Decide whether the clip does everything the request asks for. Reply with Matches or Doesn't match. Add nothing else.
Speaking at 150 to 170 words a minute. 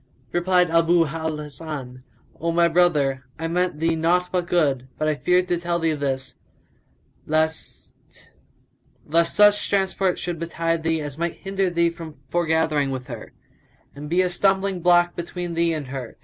Matches